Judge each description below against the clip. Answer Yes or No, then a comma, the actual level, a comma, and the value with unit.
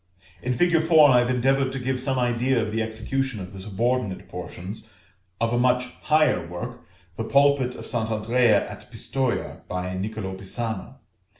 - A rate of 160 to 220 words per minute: Yes, average, 170 wpm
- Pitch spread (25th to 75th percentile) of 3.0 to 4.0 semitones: Yes, average, 3.5 semitones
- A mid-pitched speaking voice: No, low, 120 Hz